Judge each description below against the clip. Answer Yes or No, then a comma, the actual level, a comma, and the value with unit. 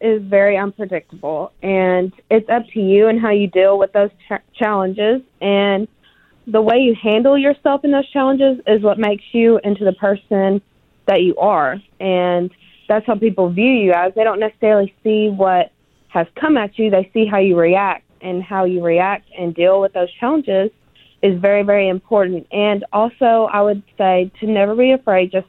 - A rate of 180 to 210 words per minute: Yes, average, 185 wpm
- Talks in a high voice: Yes, high, 205 Hz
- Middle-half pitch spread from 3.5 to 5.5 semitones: No, average, 2.7 semitones